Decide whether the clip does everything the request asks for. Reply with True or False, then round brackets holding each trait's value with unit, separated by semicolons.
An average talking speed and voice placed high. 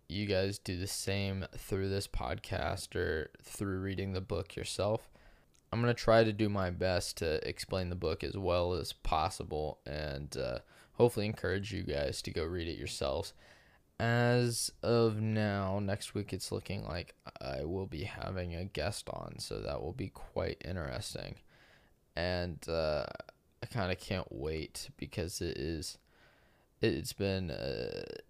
False (155 wpm; 95 Hz)